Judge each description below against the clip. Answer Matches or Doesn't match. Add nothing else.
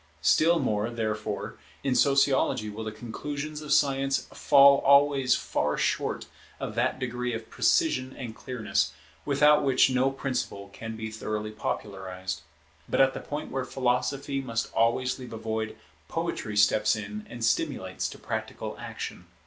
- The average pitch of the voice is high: Doesn't match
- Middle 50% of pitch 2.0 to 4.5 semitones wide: Matches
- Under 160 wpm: Matches